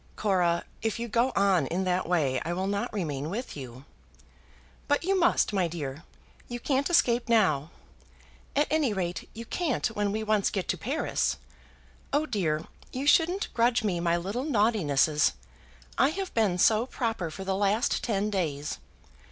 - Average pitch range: No, wide, 5.7 semitones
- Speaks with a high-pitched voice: Yes, high, 205 Hz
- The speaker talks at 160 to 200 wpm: Yes, average, 165 wpm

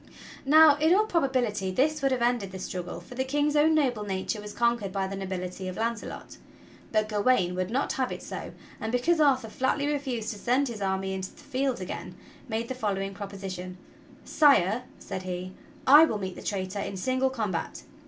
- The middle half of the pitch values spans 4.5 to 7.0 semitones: Yes, wide, 5.6 semitones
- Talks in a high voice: Yes, high, 225 Hz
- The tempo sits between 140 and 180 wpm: No, average, 195 wpm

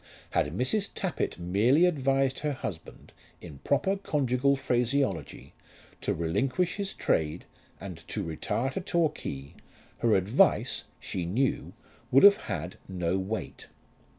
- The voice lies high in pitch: No, low, 125 Hz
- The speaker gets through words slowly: Yes, slow, 125 wpm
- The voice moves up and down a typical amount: No, wide, 8.0 semitones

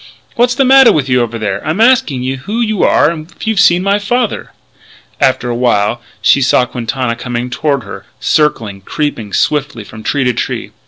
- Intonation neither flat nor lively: No, wide, 8.7 semitones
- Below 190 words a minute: No, average, 195 wpm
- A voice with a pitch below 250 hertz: Yes, low, 135 Hz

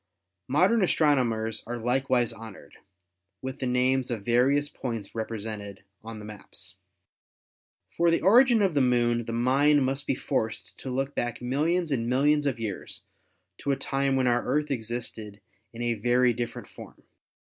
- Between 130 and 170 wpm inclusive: Yes, average, 160 wpm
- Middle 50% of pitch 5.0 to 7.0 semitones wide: No, average, 3.4 semitones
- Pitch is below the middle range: Yes, low, 125 Hz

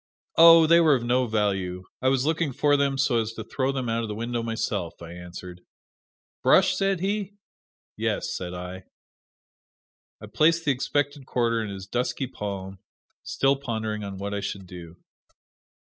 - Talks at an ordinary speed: Yes, average, 170 wpm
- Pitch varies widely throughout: Yes, wide, 6.1 semitones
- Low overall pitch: Yes, low, 115 Hz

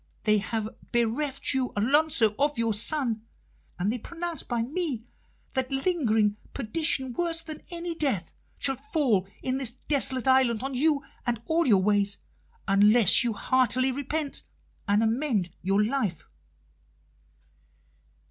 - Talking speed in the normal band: No, slow, 130 wpm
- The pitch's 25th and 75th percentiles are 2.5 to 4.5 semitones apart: No, average, 5.1 semitones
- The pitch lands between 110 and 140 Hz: No, very high, 255 Hz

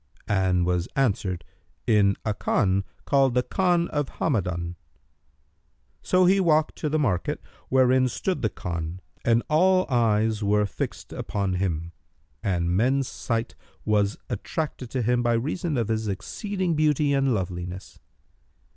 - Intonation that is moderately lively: No, wide, 6.7 semitones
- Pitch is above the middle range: No, low, 115 Hz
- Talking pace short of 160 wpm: Yes, average, 140 wpm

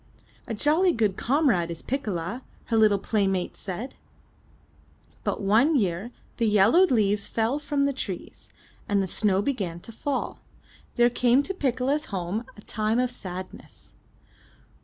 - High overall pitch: Yes, high, 225 Hz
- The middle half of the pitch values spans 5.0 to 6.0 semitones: Yes, average, 5.3 semitones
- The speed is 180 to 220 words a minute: No, average, 150 wpm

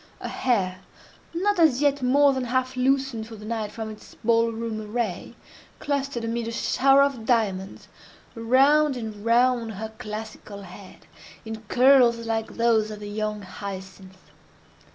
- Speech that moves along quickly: No, average, 150 wpm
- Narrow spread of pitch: No, average, 3.3 semitones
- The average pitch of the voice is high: Yes, high, 230 Hz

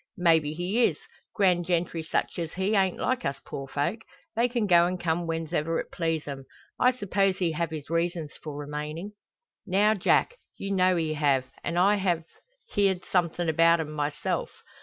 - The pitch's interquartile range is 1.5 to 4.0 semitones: Yes, average, 3.4 semitones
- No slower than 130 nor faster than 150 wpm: No, average, 175 wpm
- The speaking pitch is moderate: Yes, medium, 170 Hz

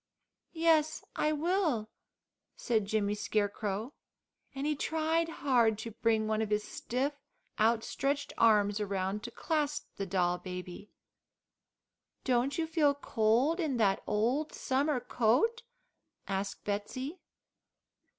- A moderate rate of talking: No, slow, 115 wpm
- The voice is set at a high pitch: Yes, high, 235 Hz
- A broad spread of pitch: Yes, wide, 6.0 semitones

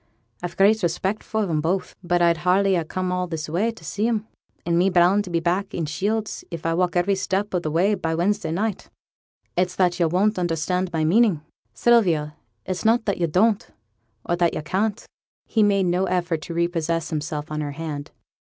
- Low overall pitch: No, medium, 180 Hz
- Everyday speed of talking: No, fast, 210 wpm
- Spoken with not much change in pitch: No, average, 3.1 semitones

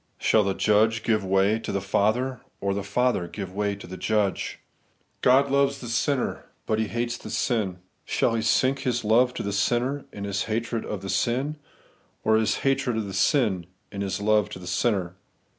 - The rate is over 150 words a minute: Yes, average, 190 wpm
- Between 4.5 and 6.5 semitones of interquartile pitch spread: No, average, 3.6 semitones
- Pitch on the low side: Yes, low, 110 Hz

